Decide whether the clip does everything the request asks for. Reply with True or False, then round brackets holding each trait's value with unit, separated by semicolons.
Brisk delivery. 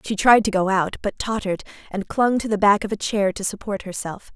True (250 wpm)